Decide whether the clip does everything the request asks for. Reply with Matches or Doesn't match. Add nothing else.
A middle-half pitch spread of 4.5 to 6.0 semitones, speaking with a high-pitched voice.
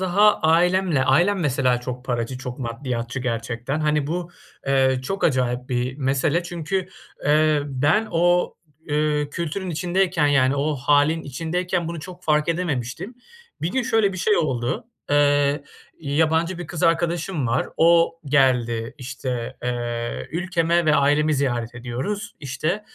Doesn't match